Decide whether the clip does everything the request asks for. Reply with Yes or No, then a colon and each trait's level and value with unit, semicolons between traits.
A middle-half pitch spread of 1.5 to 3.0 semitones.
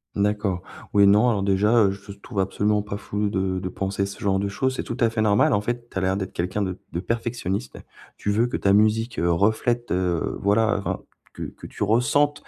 Yes: narrow, 2.6 semitones